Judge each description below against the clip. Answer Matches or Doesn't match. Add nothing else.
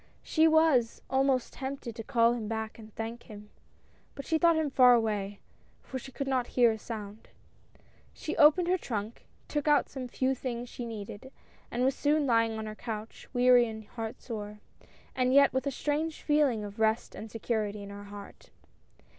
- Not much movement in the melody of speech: Doesn't match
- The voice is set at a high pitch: Matches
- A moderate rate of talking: Matches